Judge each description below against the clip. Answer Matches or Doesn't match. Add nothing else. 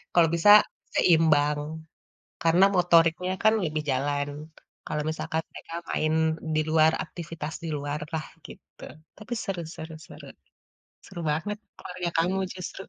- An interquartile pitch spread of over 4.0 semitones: Doesn't match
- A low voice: Doesn't match